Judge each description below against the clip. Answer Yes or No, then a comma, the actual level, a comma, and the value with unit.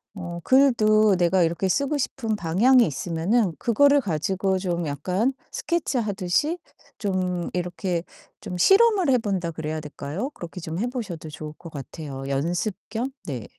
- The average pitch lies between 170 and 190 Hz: Yes, medium, 185 Hz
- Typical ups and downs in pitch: No, wide, 6.1 semitones